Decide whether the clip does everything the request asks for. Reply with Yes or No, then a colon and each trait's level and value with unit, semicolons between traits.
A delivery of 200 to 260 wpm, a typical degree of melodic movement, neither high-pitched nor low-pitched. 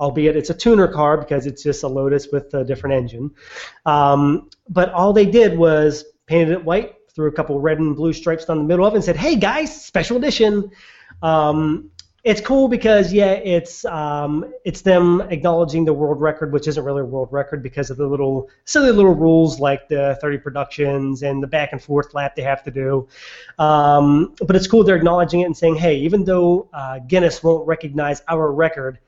Yes: fast, 205 wpm; average, 3.6 semitones; medium, 155 Hz